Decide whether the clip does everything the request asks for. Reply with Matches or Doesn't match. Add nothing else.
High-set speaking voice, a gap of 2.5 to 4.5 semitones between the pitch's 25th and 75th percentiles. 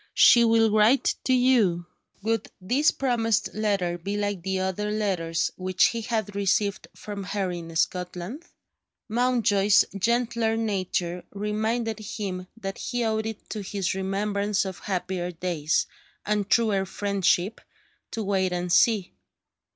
Matches